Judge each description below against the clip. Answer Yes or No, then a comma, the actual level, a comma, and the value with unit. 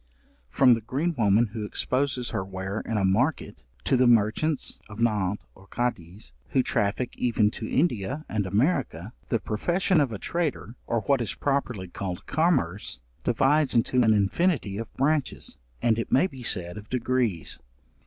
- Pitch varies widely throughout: No, average, 4.9 semitones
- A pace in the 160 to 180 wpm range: Yes, average, 165 wpm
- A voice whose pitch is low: Yes, low, 115 Hz